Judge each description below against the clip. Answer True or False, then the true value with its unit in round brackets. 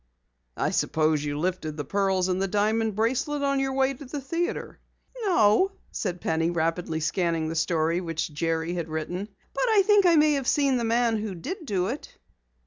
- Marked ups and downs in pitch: True (8.5 semitones)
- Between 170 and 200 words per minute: True (190 wpm)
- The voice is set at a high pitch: True (195 Hz)